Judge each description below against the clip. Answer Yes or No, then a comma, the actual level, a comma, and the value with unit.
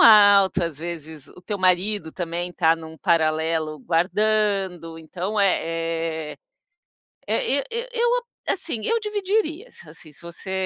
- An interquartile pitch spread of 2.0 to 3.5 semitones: No, average, 4.7 semitones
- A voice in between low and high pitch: Yes, medium, 180 Hz